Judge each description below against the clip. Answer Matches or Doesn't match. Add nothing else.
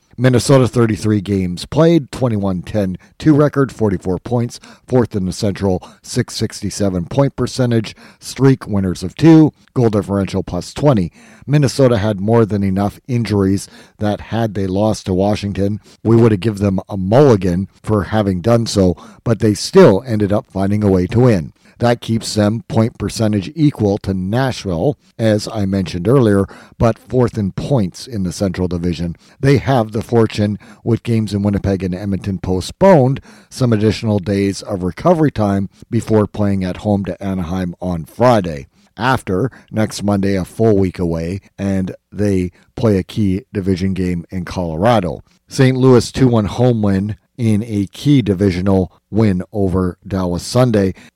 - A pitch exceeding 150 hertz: Doesn't match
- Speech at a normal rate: Matches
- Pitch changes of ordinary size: Matches